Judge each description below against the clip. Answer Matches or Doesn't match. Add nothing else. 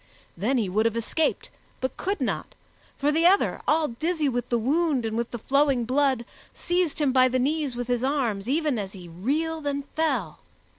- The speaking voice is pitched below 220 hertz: Doesn't match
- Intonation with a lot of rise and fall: Doesn't match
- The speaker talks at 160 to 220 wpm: Matches